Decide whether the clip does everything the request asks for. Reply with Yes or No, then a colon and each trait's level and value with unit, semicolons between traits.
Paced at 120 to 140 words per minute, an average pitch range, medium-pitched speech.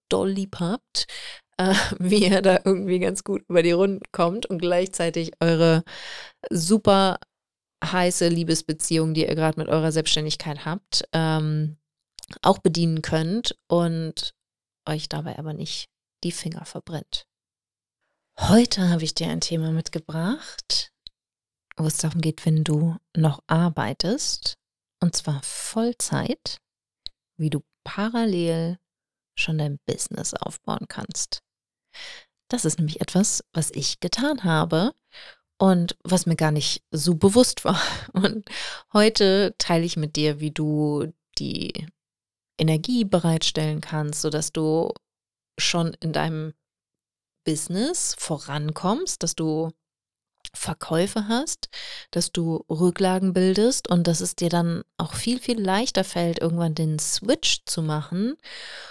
Yes: slow, 125 wpm; average, 3.3 semitones; medium, 170 Hz